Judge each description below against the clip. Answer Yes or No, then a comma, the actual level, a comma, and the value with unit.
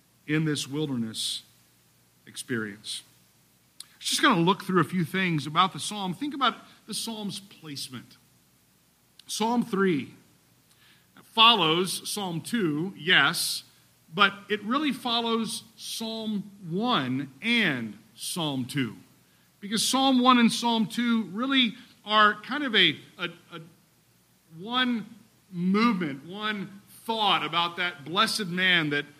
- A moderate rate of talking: No, slow, 120 wpm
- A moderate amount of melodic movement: No, wide, 7.2 semitones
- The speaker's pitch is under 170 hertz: No, medium, 185 Hz